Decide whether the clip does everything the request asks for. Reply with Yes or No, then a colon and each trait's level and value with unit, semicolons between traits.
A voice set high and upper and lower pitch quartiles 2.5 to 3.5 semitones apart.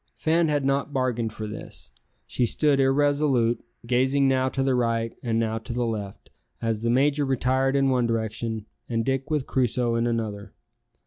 No: low, 125 Hz; average, 2.9 semitones